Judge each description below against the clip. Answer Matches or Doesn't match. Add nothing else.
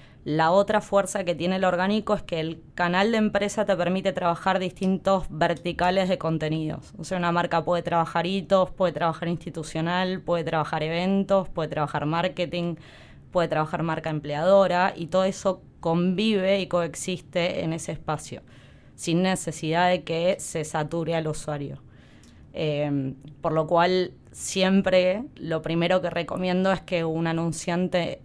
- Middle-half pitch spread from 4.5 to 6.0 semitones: Doesn't match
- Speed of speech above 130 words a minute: Matches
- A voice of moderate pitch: Matches